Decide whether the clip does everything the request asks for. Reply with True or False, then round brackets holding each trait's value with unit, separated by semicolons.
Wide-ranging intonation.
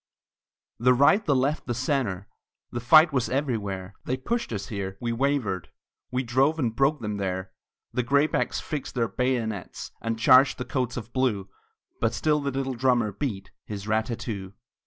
False (4.3 semitones)